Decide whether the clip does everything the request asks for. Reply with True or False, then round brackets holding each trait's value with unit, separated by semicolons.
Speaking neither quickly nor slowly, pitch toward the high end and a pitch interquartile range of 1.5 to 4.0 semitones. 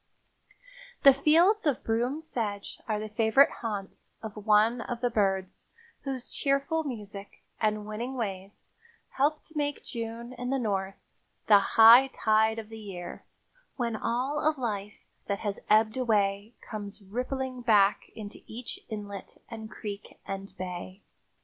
True (145 wpm; 220 Hz; 3.7 semitones)